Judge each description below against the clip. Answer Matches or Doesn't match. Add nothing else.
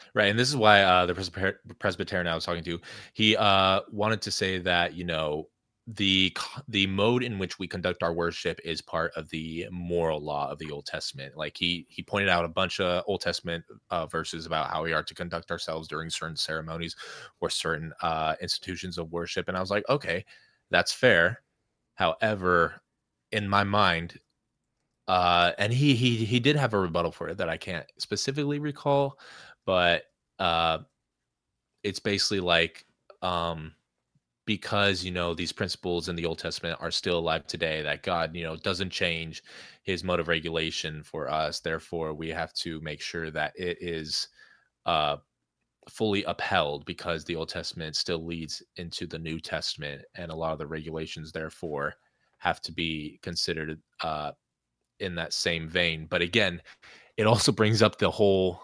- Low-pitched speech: Matches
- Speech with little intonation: Doesn't match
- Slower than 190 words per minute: Matches